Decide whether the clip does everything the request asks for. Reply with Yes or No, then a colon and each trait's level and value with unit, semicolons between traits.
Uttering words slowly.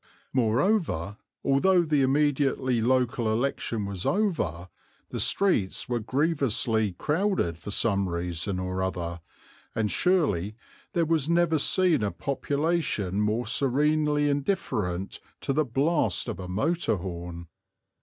Yes: slow, 120 wpm